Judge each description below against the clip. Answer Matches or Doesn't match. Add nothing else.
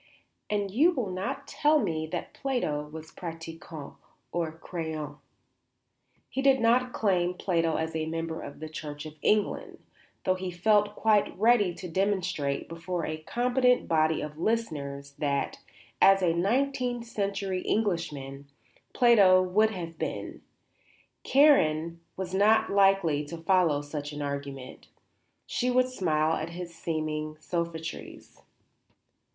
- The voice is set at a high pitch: Doesn't match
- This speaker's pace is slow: Matches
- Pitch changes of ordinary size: Matches